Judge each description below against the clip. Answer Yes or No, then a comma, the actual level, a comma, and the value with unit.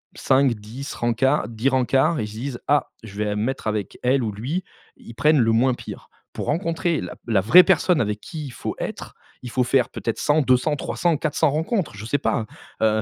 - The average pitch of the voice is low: Yes, low, 130 Hz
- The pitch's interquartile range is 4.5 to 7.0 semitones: Yes, average, 4.8 semitones